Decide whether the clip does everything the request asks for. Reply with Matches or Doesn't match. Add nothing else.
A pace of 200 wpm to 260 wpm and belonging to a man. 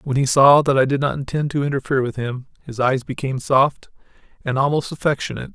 Matches